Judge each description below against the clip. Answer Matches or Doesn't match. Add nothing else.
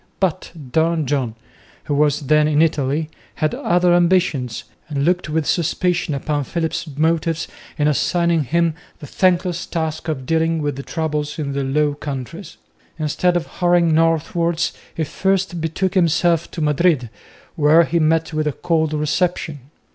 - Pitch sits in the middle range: Matches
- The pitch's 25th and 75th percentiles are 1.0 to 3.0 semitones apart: Matches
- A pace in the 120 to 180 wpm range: Matches